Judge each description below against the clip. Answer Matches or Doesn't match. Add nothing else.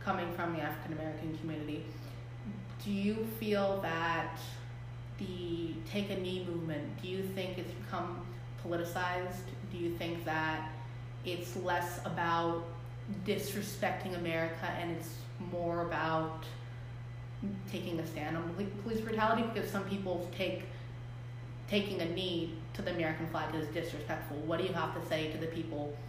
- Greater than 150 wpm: Doesn't match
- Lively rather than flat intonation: Matches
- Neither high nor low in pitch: Matches